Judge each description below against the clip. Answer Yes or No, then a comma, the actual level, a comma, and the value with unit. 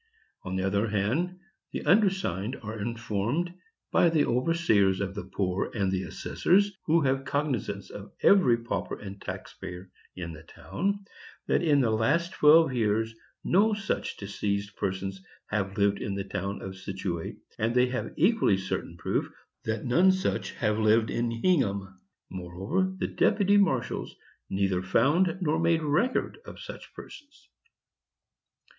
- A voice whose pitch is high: No, low, 115 Hz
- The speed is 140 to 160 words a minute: Yes, average, 150 wpm